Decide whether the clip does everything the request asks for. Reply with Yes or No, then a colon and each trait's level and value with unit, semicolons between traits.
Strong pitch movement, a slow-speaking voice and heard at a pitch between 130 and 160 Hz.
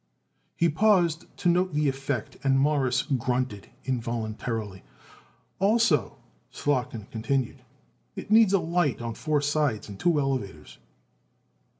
Yes: wide, 6.1 semitones; slow, 115 wpm; low, 135 Hz